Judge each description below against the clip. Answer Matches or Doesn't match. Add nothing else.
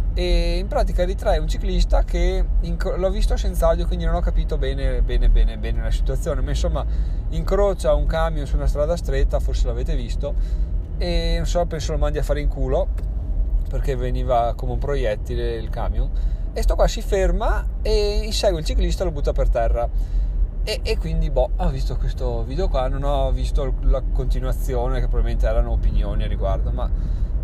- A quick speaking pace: Matches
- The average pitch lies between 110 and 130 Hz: Matches